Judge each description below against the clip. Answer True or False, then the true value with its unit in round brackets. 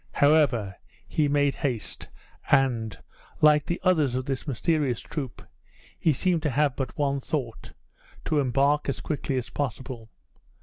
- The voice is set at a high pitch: False (140 Hz)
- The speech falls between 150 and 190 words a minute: False (140 wpm)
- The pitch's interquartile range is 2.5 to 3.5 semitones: True (2.8 semitones)